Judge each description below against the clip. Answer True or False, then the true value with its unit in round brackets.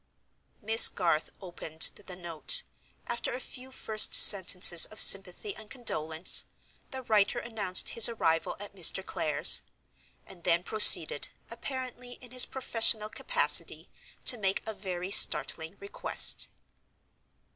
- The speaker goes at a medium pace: False (125 wpm)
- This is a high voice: True (205 Hz)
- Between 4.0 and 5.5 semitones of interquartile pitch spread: True (4.6 semitones)